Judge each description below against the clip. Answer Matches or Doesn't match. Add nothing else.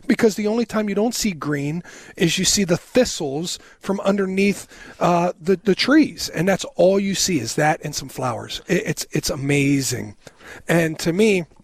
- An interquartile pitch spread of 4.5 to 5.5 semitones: Matches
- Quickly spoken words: Doesn't match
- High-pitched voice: Doesn't match